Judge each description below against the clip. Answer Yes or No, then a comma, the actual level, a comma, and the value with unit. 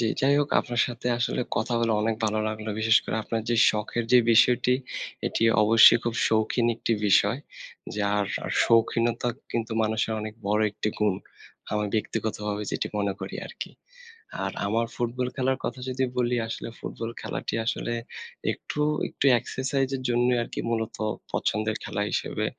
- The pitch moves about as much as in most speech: No, narrow, 2.2 semitones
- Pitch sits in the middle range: No, low, 115 Hz